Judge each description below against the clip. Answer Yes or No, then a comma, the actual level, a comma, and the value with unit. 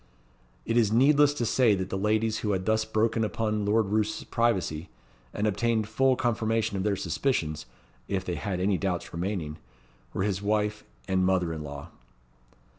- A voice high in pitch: No, low, 105 Hz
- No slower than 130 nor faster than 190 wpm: Yes, average, 170 wpm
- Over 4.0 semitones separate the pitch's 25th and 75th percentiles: No, average, 3.1 semitones